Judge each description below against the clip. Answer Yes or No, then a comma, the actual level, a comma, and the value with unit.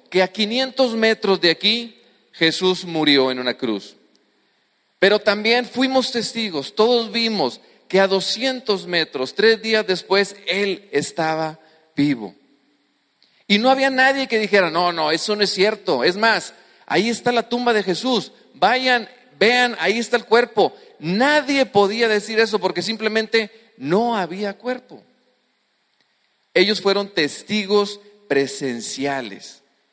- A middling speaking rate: No, slow, 130 wpm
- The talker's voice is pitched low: No, high, 210 Hz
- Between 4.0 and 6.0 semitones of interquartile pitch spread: Yes, average, 4.5 semitones